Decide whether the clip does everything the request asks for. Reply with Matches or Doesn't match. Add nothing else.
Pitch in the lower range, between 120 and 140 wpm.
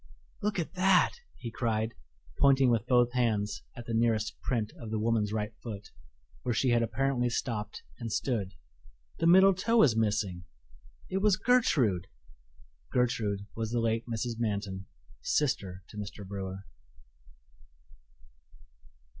Matches